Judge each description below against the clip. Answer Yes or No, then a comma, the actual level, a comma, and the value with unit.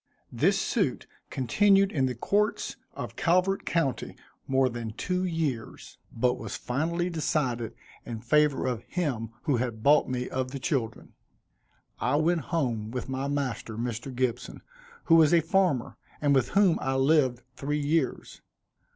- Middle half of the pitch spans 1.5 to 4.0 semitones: No, average, 5.1 semitones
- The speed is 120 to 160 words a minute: Yes, average, 150 wpm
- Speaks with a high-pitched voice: No, low, 135 Hz